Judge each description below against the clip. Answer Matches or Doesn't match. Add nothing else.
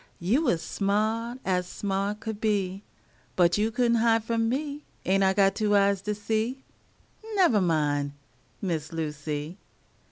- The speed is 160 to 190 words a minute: Doesn't match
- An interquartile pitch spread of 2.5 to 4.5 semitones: Matches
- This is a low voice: Doesn't match